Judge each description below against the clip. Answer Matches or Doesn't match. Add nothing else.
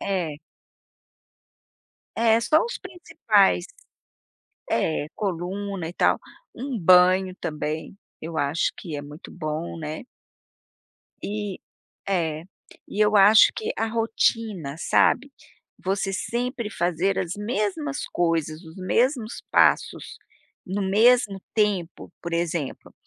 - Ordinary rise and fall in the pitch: Matches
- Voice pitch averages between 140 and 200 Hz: Matches